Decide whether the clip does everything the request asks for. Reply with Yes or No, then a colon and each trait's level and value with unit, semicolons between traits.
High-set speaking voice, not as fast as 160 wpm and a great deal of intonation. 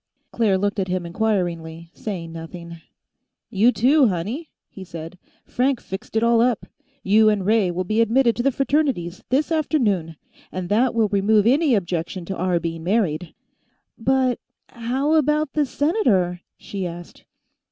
Yes: high, 210 Hz; average, 150 wpm; wide, 6.1 semitones